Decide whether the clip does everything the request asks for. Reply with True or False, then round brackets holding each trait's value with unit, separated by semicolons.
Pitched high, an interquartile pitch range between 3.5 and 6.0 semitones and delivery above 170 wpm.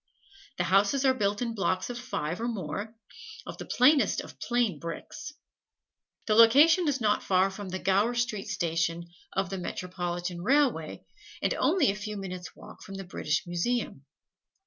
False (200 Hz; 5.2 semitones; 165 wpm)